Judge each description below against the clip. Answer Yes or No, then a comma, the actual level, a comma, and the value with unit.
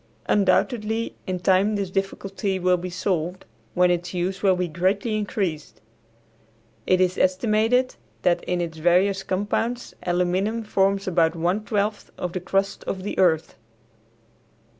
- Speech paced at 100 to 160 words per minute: Yes, average, 140 wpm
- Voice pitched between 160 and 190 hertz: Yes, medium, 185 Hz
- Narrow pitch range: Yes, narrow, 2.2 semitones